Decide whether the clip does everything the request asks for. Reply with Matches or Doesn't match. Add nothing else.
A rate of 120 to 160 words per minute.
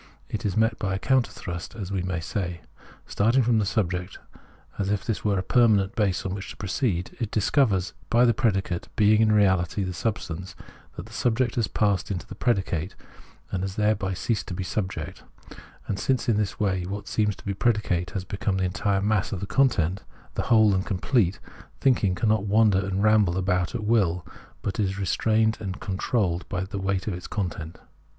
Doesn't match